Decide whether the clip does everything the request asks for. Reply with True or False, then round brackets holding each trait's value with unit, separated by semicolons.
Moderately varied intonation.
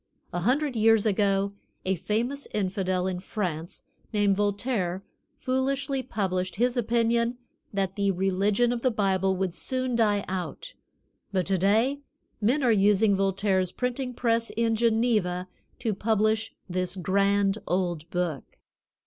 True (3.7 semitones)